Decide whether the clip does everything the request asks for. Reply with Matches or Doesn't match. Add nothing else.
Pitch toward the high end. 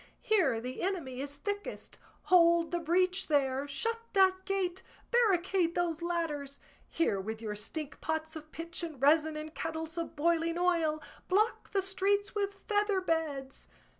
Matches